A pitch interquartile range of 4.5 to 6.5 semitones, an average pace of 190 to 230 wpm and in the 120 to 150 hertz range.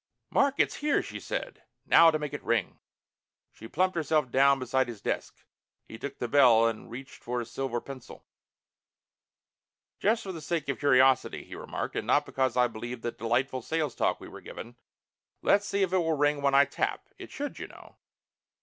Yes: average, 4.9 semitones; average, 195 wpm; low, 135 Hz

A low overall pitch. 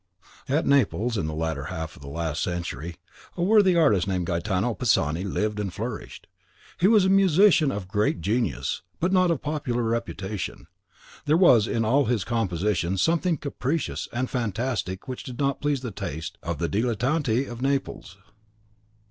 Yes: low, 115 Hz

